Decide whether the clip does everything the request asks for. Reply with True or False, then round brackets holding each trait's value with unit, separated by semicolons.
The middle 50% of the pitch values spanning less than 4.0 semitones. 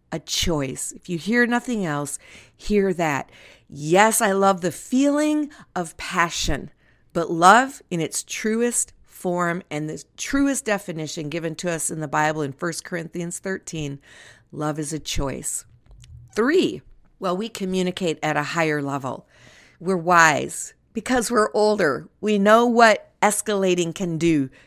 False (5.2 semitones)